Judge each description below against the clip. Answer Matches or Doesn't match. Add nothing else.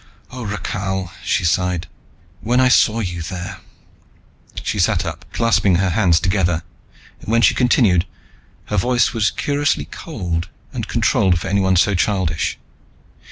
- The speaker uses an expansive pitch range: Doesn't match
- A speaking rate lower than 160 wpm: Matches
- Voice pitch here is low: Matches